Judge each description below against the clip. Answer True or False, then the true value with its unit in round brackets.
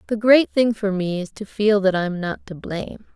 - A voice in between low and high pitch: False (205 Hz)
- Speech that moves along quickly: True (250 wpm)